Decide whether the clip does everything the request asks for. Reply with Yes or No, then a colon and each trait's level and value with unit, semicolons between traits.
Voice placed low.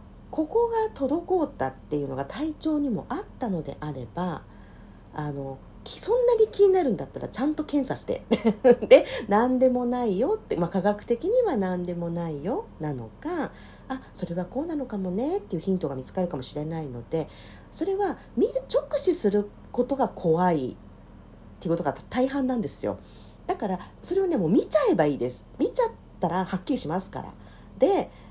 No: high, 210 Hz